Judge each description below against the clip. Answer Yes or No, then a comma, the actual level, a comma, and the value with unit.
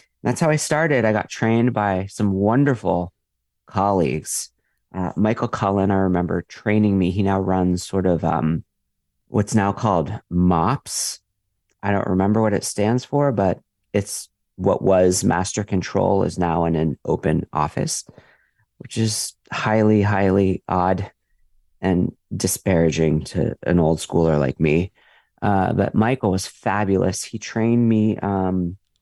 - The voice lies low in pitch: Yes, very low, 95 Hz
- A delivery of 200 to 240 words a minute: No, average, 145 wpm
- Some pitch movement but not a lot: Yes, average, 3.3 semitones